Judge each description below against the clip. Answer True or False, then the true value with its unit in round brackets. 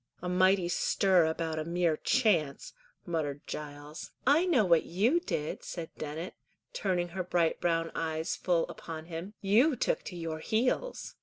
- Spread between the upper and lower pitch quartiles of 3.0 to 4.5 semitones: True (3.4 semitones)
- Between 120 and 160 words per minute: True (155 wpm)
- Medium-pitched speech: True (175 Hz)